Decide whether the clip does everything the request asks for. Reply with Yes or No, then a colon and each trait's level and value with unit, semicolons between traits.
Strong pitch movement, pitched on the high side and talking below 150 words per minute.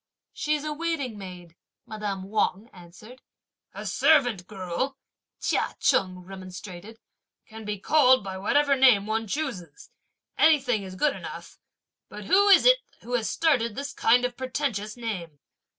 Yes: wide, 6.2 semitones; high, 225 Hz; slow, 135 wpm